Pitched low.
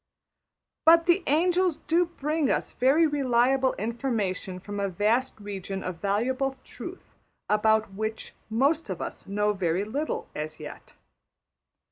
No: high, 230 Hz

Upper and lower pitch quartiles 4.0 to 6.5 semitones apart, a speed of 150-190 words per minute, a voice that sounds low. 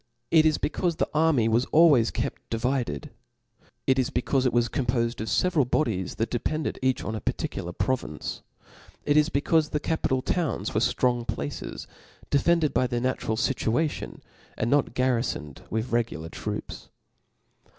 Yes: average, 4.5 semitones; average, 155 wpm; low, 130 Hz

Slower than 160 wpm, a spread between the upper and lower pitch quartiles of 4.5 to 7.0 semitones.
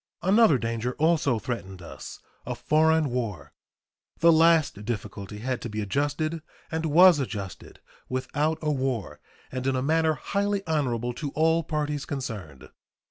Yes: average, 140 wpm; wide, 5.6 semitones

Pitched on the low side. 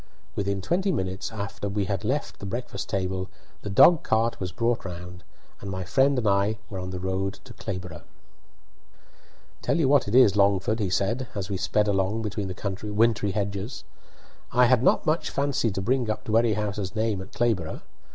Yes: low, 100 Hz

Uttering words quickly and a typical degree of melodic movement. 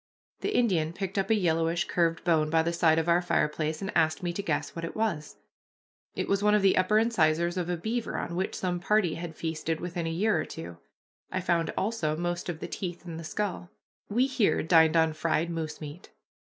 Yes: fast, 220 wpm; average, 3.0 semitones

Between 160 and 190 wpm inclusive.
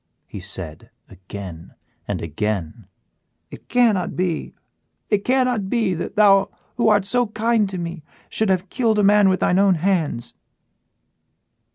No: average, 145 wpm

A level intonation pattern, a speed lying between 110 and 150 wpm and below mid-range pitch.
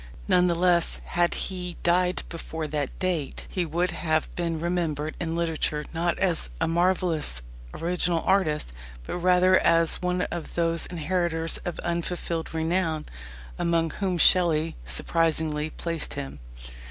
No: narrow, 1.8 semitones; slow, 135 wpm; medium, 170 Hz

